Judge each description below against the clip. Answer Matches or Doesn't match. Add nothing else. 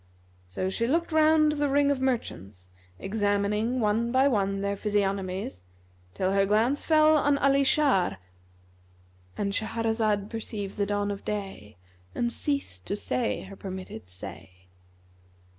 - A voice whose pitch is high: Matches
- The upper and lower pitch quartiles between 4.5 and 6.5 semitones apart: Matches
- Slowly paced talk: Matches